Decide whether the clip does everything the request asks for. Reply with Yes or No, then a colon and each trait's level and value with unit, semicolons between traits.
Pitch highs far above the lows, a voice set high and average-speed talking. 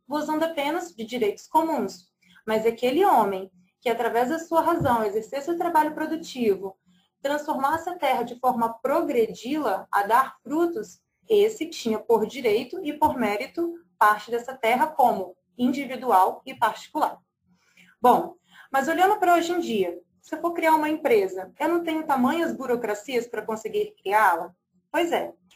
Yes: wide, 6.6 semitones; very high, 265 Hz; average, 150 wpm